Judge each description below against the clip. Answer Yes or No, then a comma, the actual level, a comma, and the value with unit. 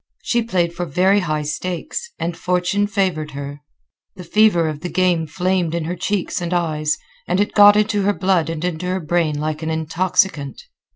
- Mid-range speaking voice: Yes, medium, 175 Hz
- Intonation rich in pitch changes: No, average, 3.1 semitones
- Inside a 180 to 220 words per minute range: Yes, average, 185 wpm